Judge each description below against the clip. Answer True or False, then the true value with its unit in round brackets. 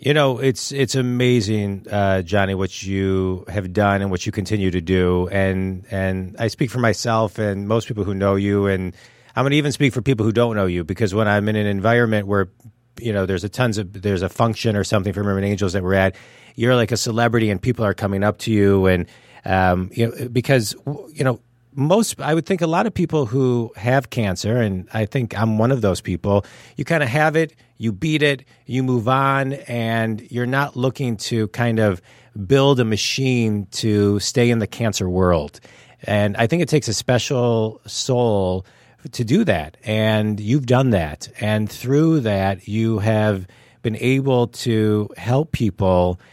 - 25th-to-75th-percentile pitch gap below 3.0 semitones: False (4.0 semitones)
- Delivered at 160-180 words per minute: False (200 wpm)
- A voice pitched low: True (110 Hz)